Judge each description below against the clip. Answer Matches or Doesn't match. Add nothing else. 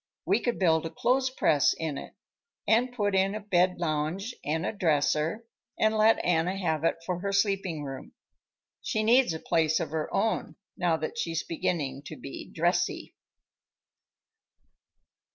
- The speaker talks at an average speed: Matches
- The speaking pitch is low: Doesn't match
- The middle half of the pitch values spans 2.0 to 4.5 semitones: Doesn't match